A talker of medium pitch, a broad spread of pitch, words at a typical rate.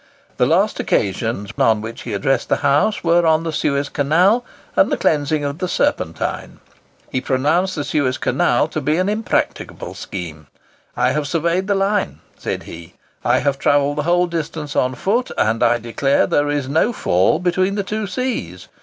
Yes: medium, 150 Hz; wide, 5.8 semitones; average, 180 wpm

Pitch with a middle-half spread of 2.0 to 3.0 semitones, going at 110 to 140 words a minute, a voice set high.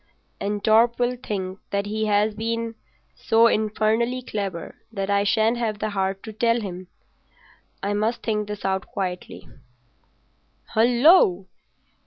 Yes: narrow, 2.4 semitones; slow, 135 wpm; high, 215 Hz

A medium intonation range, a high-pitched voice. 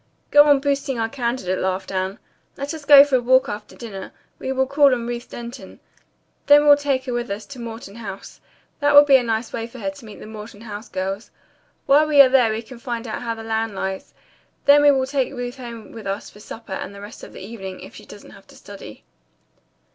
Yes: average, 4.3 semitones; high, 235 Hz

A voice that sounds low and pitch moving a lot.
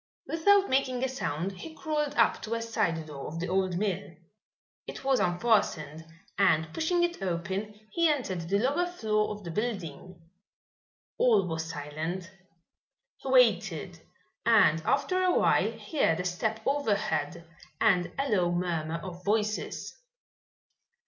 No: high, 200 Hz; wide, 7.3 semitones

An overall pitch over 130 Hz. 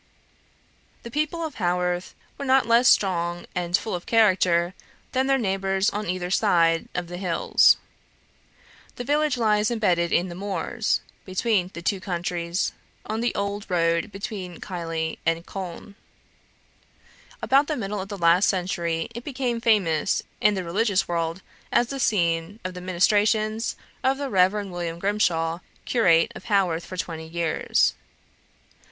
Yes: high, 190 Hz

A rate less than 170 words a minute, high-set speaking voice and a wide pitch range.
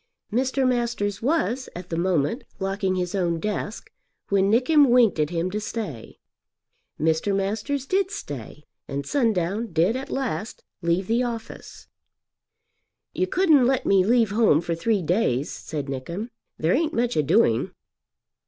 Yes: average, 145 wpm; high, 205 Hz; wide, 6.4 semitones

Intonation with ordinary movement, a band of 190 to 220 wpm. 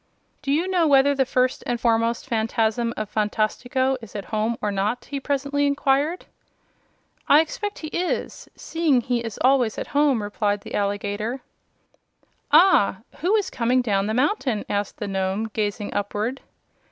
No: average, 4.9 semitones; average, 160 wpm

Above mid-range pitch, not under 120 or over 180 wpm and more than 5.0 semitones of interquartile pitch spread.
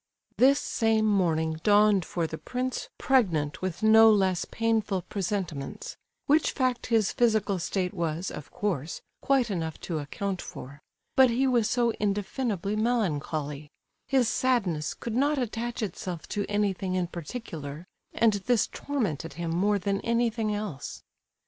Yes: high, 205 Hz; slow, 135 wpm; wide, 5.4 semitones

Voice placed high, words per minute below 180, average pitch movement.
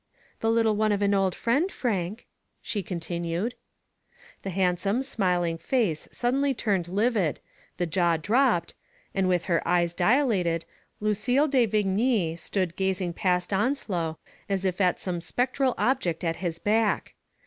Yes: high, 195 Hz; average, 140 wpm; average, 4.7 semitones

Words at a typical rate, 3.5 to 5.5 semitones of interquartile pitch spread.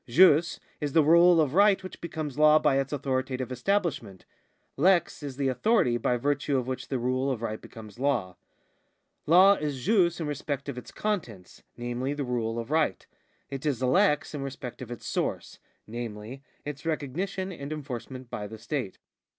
Yes: average, 175 wpm; average, 4.2 semitones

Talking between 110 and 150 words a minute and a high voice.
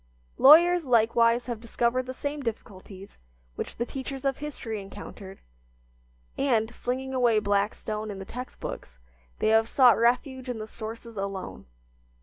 Yes: average, 140 wpm; high, 235 Hz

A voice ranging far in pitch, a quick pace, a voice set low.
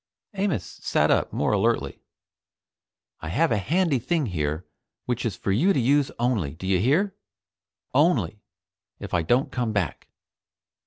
No: wide, 7.7 semitones; average, 150 wpm; low, 120 Hz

